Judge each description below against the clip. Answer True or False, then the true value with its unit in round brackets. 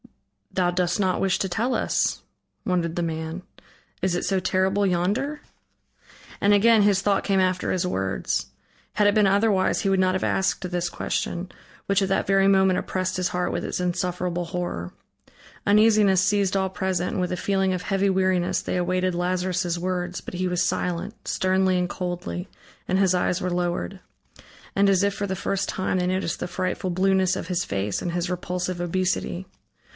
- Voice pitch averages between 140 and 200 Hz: True (185 Hz)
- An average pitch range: False (1.5 semitones)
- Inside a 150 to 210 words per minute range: True (185 wpm)